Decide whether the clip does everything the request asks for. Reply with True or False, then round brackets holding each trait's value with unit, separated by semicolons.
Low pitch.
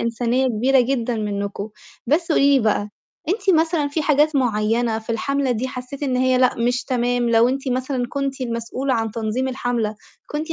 False (250 Hz)